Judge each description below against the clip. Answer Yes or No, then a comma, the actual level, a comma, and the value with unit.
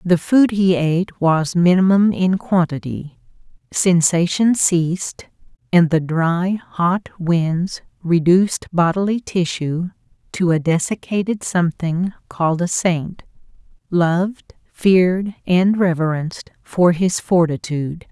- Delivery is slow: Yes, slow, 105 wpm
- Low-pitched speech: No, medium, 175 Hz